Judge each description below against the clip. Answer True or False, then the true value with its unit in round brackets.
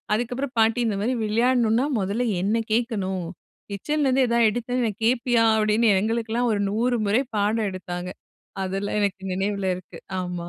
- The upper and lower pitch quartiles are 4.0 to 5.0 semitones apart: False (3.4 semitones)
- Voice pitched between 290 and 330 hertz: False (220 Hz)